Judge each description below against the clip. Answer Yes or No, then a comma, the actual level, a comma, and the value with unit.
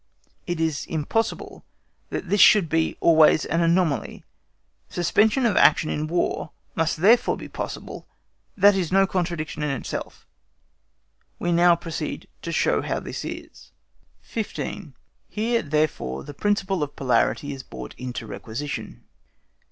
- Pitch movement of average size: Yes, average, 4.4 semitones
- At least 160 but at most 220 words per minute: No, slow, 135 wpm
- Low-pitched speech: No, medium, 165 Hz